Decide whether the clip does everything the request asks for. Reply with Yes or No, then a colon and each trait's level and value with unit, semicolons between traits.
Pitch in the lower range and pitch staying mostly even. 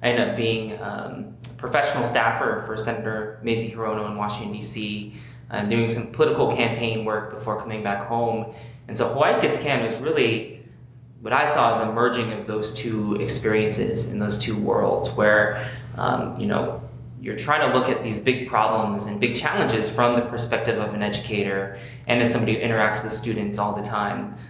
Yes: low, 110 Hz; narrow, 1.9 semitones